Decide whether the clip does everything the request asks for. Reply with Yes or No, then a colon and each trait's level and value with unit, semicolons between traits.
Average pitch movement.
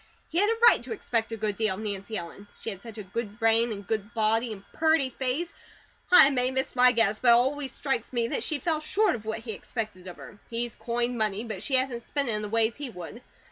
Yes: average, 3.4 semitones